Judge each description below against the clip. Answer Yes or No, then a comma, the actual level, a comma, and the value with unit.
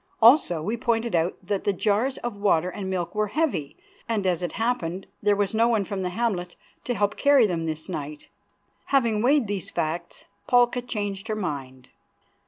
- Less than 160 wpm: No, average, 190 wpm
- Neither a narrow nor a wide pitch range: Yes, average, 4.7 semitones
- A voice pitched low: No, high, 205 Hz